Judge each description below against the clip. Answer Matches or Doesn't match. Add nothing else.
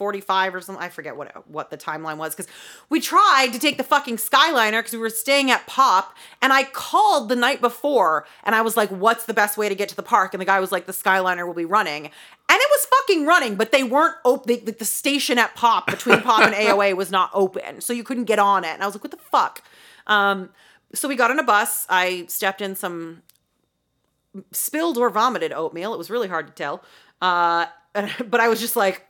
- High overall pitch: Matches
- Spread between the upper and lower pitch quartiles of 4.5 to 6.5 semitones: Matches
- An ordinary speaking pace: Doesn't match